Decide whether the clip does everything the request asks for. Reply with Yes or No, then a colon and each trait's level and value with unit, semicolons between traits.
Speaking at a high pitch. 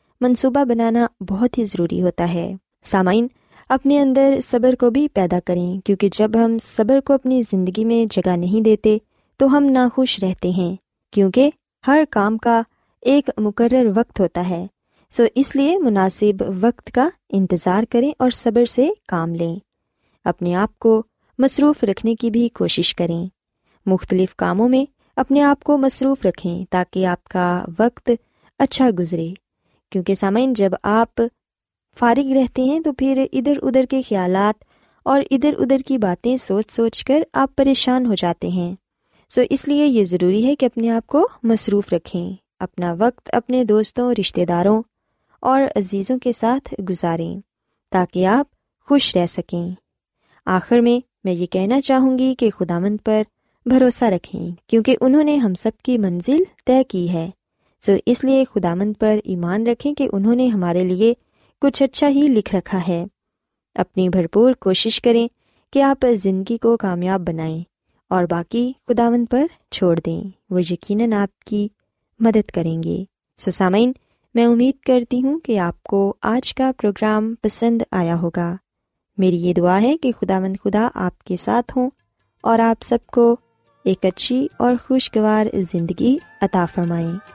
Yes: high, 225 Hz